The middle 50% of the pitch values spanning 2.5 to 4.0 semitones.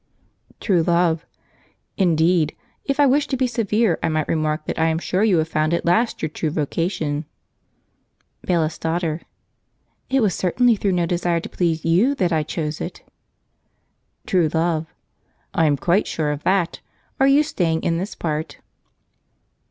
Yes: average, 3.5 semitones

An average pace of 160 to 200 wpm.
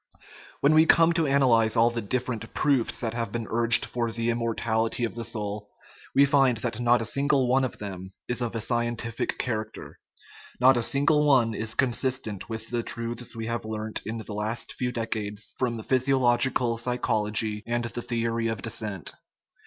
Yes: average, 180 wpm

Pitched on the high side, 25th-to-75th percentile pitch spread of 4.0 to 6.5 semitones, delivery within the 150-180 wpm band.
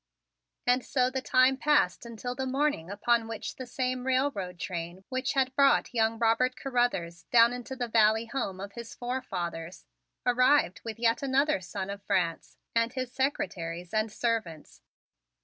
Yes: high, 235 Hz; average, 4.7 semitones; average, 155 wpm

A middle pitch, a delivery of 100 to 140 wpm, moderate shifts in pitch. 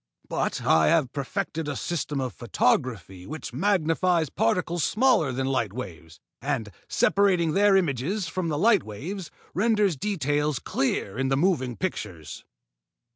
No: medium, 150 Hz; slow, 135 wpm; wide, 6.5 semitones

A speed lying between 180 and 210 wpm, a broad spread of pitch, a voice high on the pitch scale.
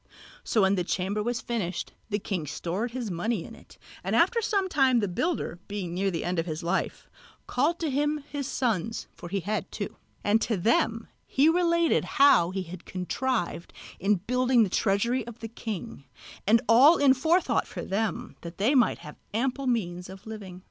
Yes: average, 190 wpm; wide, 5.8 semitones; high, 220 Hz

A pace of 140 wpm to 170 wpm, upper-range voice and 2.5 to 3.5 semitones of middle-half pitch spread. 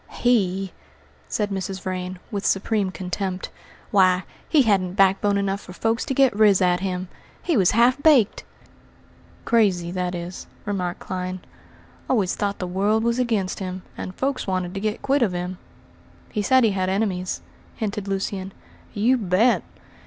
Yes: average, 155 wpm; high, 195 Hz; average, 3.1 semitones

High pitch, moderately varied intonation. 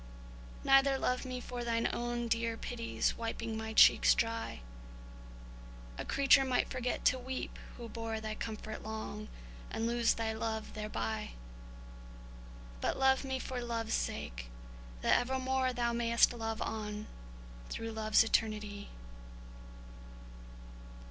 No: high, 230 Hz; narrow, 2.1 semitones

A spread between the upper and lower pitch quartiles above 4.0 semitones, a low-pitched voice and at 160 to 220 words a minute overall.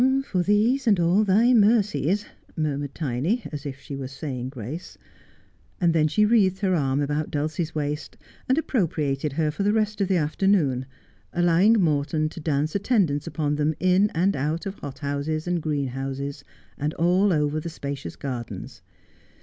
No: average, 5.2 semitones; medium, 155 Hz; average, 170 wpm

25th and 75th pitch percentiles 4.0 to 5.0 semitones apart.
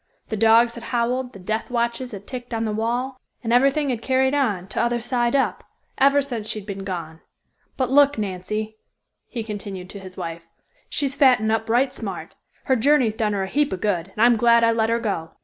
No: average, 3.4 semitones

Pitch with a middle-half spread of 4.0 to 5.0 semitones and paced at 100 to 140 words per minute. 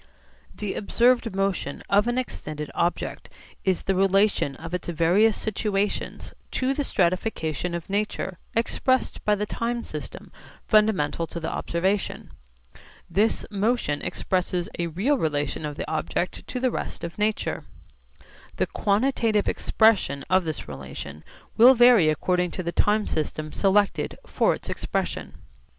Yes: average, 4.6 semitones; slow, 135 wpm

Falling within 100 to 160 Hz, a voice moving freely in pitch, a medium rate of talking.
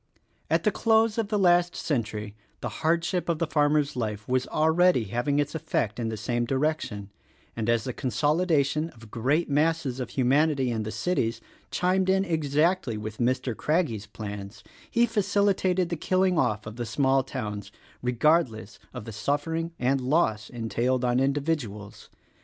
Yes: low, 135 Hz; wide, 6.3 semitones; average, 165 wpm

